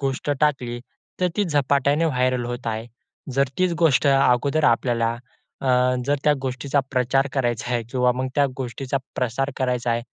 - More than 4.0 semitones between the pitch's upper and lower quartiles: No, narrow, 2.5 semitones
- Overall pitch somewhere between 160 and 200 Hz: No, low, 130 Hz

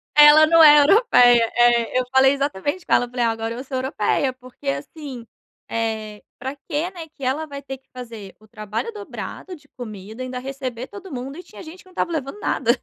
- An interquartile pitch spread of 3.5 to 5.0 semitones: Yes, average, 4.4 semitones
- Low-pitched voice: No, very high, 260 Hz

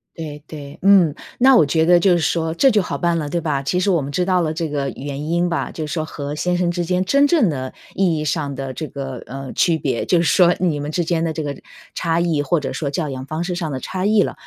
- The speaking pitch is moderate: Yes, medium, 160 Hz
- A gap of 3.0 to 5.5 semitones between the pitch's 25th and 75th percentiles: Yes, average, 3.4 semitones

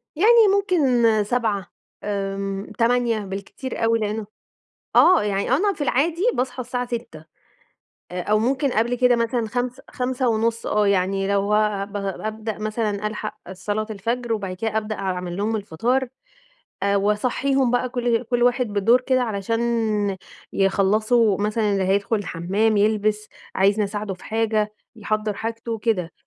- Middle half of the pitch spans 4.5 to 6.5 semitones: No, average, 3.2 semitones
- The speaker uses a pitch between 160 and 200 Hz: No, high, 215 Hz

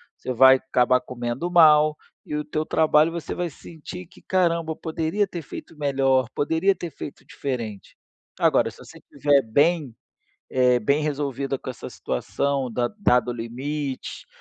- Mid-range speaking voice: Yes, medium, 145 Hz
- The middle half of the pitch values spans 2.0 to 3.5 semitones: No, average, 3.9 semitones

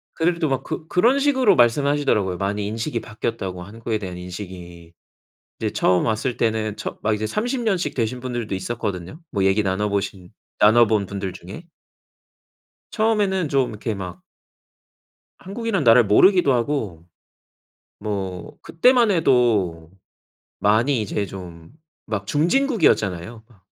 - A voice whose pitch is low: Yes, low, 110 Hz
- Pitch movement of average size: No, wide, 7.1 semitones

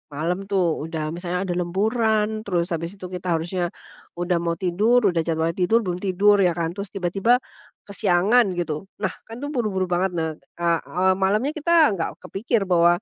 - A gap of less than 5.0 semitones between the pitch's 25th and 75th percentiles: Yes, average, 3.2 semitones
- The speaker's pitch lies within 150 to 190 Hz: Yes, medium, 185 Hz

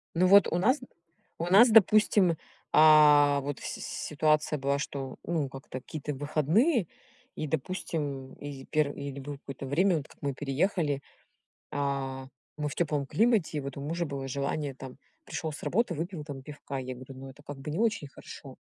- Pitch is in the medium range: Yes, medium, 145 Hz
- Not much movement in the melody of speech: No, average, 3.5 semitones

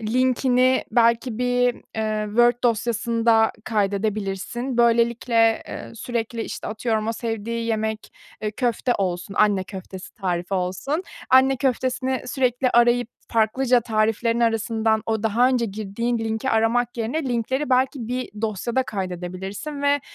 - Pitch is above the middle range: Yes, high, 230 Hz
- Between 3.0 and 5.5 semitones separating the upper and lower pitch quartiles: No, narrow, 2.4 semitones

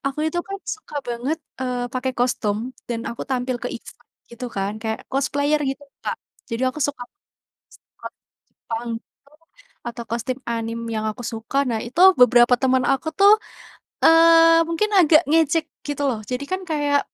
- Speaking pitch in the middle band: No, very high, 260 Hz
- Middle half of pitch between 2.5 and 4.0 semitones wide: No, average, 4.4 semitones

